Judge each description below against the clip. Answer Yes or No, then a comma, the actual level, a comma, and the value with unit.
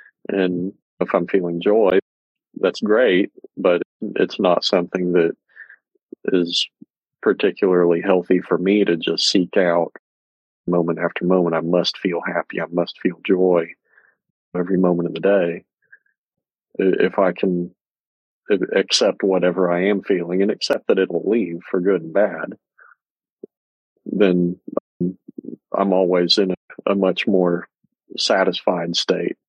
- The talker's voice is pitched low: Yes, very low, 90 Hz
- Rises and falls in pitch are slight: Yes, narrow, 1.4 semitones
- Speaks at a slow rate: Yes, slow, 130 wpm